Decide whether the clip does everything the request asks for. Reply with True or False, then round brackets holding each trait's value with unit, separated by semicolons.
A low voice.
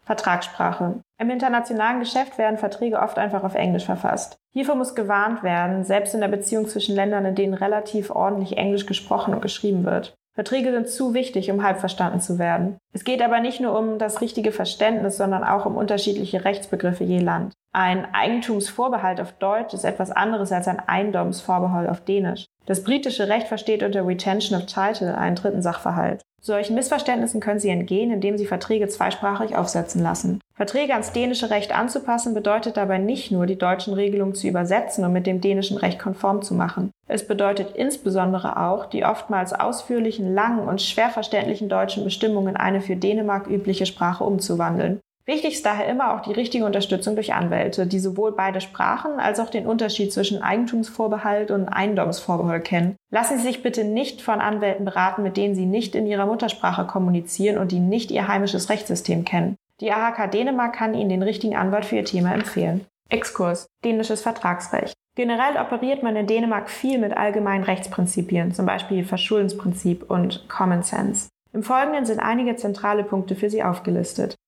False (205 Hz)